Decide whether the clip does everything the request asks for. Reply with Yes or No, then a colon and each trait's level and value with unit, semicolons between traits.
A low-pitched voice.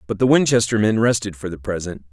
Yes: low, 100 Hz